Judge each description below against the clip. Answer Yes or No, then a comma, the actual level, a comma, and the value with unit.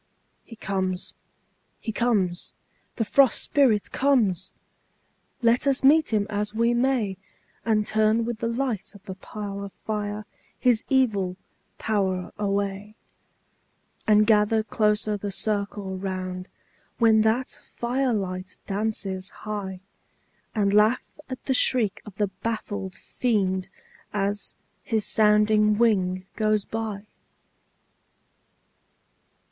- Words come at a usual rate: No, slow, 110 wpm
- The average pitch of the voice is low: No, high, 210 Hz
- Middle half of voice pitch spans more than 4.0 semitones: No, narrow, 2.4 semitones